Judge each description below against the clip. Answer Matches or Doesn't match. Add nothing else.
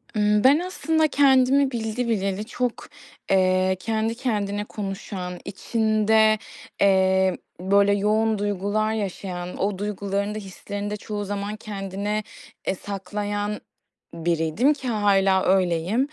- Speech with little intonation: Matches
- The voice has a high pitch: Matches